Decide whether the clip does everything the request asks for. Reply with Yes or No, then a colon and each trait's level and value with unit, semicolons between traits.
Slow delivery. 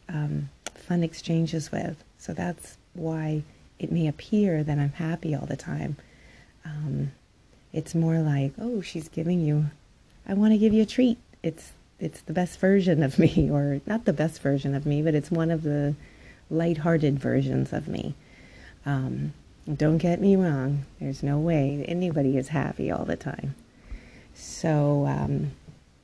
No: average, 160 wpm